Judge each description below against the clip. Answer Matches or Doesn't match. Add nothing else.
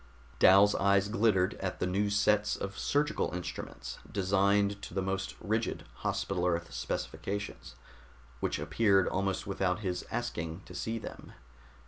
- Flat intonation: Matches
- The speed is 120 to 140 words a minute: Matches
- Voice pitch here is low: Matches